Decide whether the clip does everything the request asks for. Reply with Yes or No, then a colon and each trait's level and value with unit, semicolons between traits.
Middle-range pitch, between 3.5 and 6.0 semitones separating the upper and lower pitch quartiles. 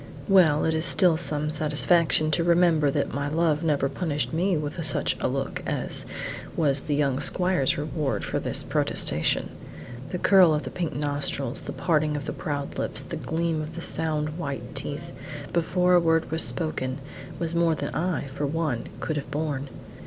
No: medium, 155 Hz; narrow, 2.6 semitones